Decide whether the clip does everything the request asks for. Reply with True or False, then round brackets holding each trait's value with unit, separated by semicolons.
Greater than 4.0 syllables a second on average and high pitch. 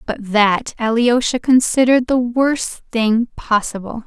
False (3.9 syllables/s; 235 Hz)